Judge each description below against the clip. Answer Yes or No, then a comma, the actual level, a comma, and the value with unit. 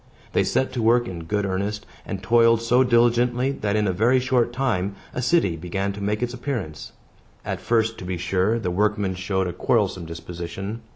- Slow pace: No, average, 190 wpm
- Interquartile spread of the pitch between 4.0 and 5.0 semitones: Yes, average, 4.3 semitones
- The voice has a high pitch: No, low, 105 Hz